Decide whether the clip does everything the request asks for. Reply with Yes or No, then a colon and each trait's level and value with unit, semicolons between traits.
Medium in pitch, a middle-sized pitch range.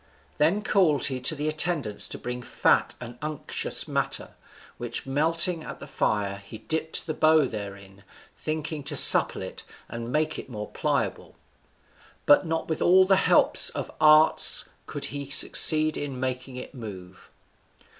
Yes: medium, 145 Hz; average, 4.7 semitones